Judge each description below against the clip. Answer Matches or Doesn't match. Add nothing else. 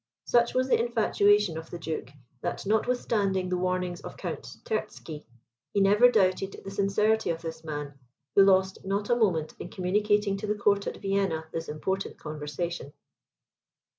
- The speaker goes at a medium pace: Matches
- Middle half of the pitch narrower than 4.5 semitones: Matches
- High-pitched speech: Matches